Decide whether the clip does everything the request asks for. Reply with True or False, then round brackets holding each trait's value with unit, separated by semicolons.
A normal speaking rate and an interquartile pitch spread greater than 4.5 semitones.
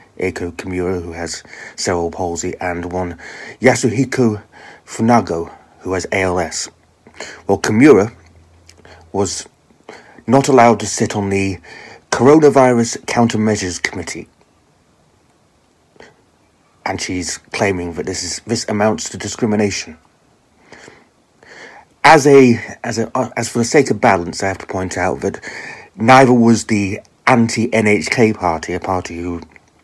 False (120 wpm; 5.0 semitones)